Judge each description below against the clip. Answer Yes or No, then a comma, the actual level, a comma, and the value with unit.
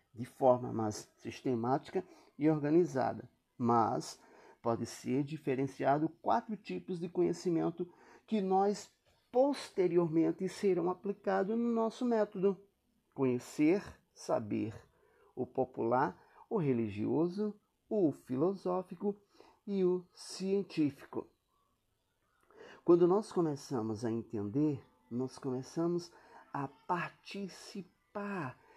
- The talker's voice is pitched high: No, medium, 175 Hz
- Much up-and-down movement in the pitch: Yes, wide, 6.7 semitones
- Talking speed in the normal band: No, slow, 90 wpm